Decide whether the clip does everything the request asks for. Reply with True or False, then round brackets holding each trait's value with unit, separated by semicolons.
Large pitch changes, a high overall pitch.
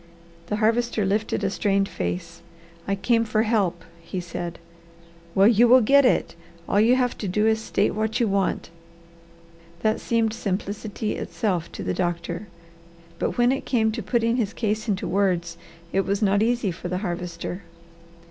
False (3.4 semitones; 210 Hz)